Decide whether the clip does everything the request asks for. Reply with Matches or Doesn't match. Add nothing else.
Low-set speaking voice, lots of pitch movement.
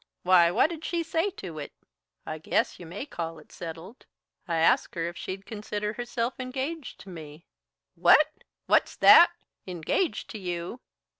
Doesn't match